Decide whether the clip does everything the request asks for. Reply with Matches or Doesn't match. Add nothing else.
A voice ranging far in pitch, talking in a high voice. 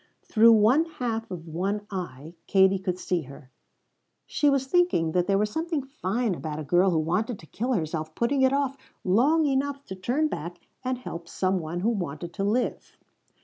Matches